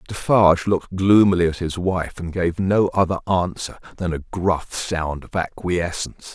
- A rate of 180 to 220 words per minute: No, average, 160 wpm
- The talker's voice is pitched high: No, very low, 90 Hz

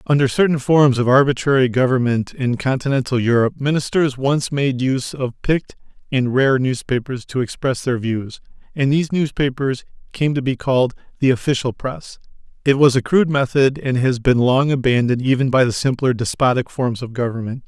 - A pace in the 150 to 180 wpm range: Yes, average, 170 wpm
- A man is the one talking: Yes, male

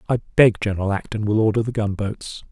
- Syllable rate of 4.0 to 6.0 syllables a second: Yes, 5.7 syllables/s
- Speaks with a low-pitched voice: Yes, low, 105 Hz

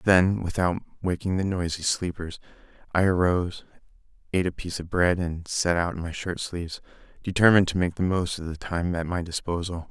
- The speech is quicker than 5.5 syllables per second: Yes, 5.7 syllables/s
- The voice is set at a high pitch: No, very low, 90 Hz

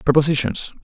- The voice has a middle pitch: Yes, medium, 145 Hz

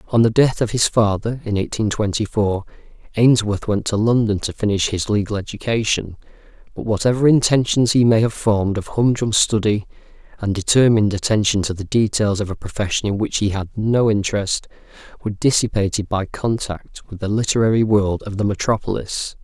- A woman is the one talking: No, male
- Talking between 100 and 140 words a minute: No, average, 170 wpm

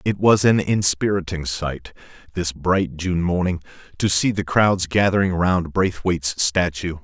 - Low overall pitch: Yes, very low, 90 Hz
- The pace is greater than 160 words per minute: No, average, 145 wpm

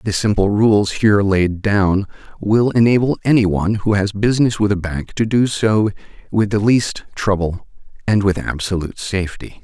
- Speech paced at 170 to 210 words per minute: No, average, 160 wpm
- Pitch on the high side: No, low, 100 Hz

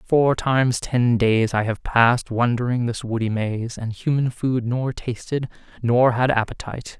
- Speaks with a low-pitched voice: Yes, low, 120 Hz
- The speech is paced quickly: No, average, 165 wpm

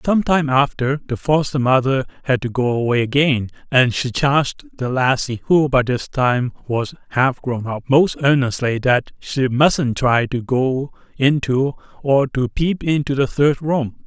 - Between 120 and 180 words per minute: Yes, average, 170 wpm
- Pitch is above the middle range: No, low, 135 Hz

